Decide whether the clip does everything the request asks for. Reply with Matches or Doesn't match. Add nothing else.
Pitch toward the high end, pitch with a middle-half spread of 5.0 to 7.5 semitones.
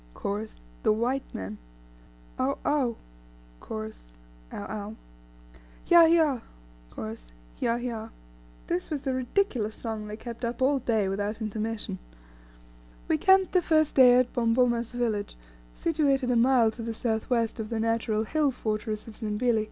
Doesn't match